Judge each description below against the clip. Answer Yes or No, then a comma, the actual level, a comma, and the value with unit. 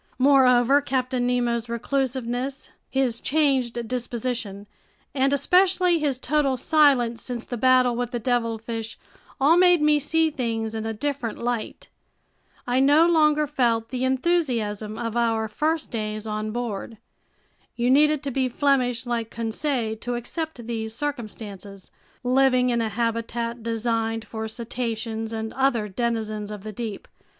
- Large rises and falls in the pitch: No, average, 3.2 semitones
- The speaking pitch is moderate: No, high, 240 Hz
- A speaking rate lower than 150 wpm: Yes, average, 140 wpm